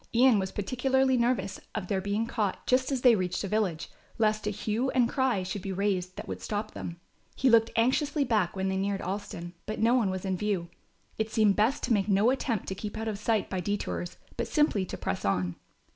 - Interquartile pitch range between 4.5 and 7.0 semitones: No, average, 3.7 semitones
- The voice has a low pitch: No, high, 210 Hz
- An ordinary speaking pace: No, fast, 220 wpm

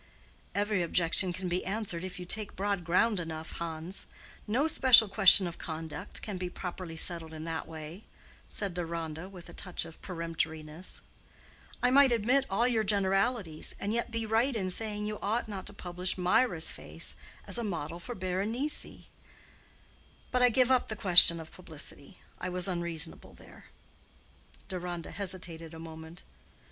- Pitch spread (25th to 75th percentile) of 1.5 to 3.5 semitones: No, average, 4.2 semitones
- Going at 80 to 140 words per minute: No, average, 160 wpm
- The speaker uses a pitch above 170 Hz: Yes, medium, 185 Hz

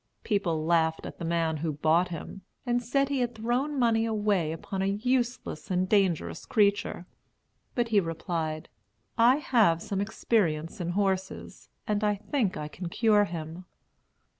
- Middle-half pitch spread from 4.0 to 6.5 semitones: Yes, average, 5.2 semitones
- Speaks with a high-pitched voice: Yes, high, 195 Hz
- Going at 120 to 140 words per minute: No, average, 155 wpm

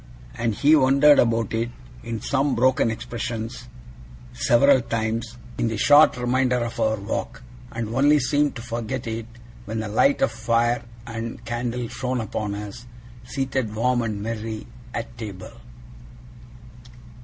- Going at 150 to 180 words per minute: No, average, 140 wpm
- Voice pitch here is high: No, low, 115 Hz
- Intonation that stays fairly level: Yes, narrow, 2.1 semitones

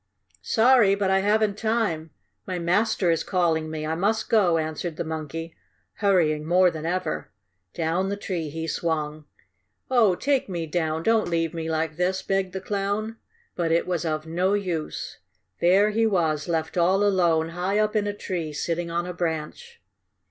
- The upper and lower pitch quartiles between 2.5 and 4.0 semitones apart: Yes, average, 3.7 semitones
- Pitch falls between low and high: Yes, medium, 175 Hz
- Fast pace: No, average, 170 wpm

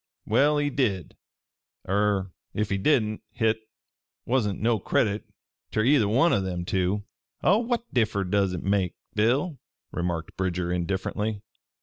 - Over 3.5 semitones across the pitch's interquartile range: Yes, average, 4.4 semitones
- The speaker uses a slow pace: Yes, slow, 130 wpm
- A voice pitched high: No, low, 105 Hz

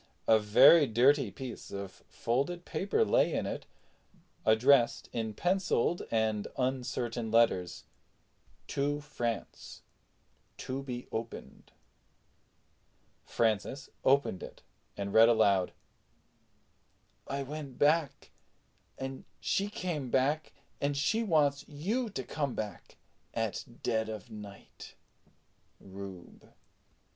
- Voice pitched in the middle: No, low, 130 Hz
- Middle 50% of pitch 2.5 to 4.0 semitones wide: No, average, 4.8 semitones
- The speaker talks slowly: Yes, slow, 100 wpm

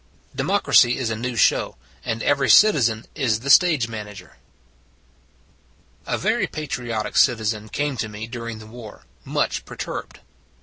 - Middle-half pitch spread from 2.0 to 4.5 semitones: Yes, average, 3.3 semitones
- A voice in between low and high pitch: No, low, 115 Hz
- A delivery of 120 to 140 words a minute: Yes, slow, 135 wpm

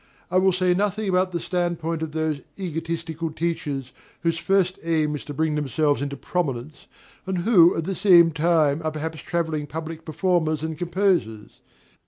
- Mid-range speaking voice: Yes, medium, 165 Hz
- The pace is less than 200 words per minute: Yes, average, 170 wpm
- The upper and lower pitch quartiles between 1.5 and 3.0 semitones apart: Yes, narrow, 2.5 semitones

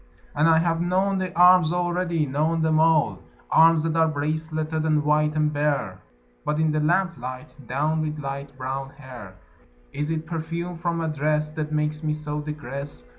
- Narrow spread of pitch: Yes, narrow, 1.8 semitones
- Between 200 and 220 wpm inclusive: No, average, 175 wpm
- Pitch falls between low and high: Yes, medium, 155 Hz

